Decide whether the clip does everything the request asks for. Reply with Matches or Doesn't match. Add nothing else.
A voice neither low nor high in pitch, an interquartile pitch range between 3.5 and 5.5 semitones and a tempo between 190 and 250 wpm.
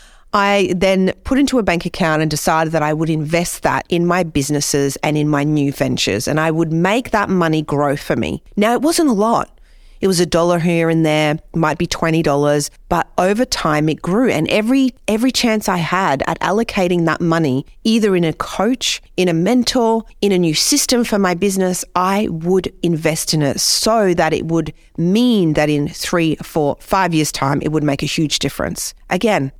Matches